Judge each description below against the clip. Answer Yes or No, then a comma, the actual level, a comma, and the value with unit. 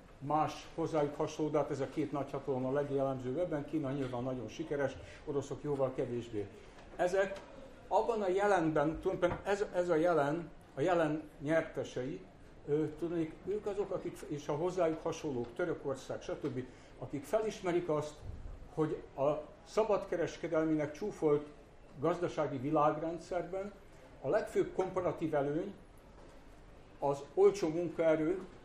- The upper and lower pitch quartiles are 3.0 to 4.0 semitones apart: Yes, average, 3.5 semitones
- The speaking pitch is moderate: Yes, medium, 155 Hz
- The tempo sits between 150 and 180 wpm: No, average, 120 wpm